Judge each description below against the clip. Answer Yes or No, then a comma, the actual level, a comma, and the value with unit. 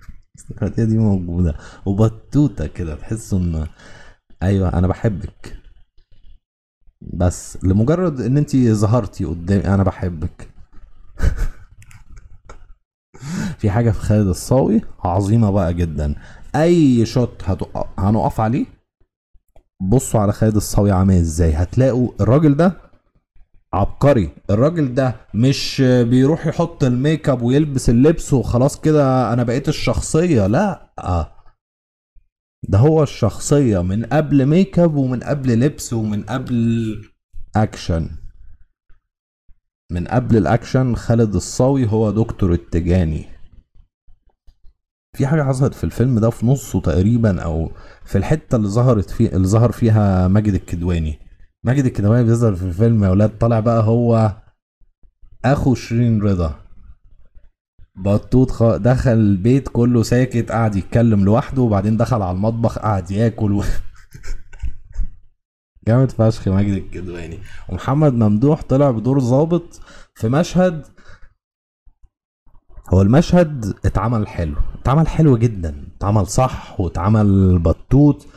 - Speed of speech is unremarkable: Yes, average, 115 wpm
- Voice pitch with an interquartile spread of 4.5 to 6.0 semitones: Yes, wide, 5.4 semitones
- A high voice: No, low, 105 Hz